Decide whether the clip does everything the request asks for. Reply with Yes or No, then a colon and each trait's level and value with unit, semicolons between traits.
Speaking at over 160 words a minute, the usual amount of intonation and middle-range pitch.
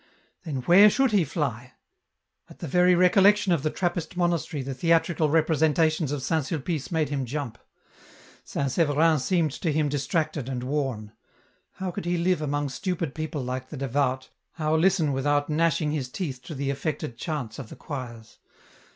Yes: average, 170 wpm; average, 3.7 semitones; medium, 150 Hz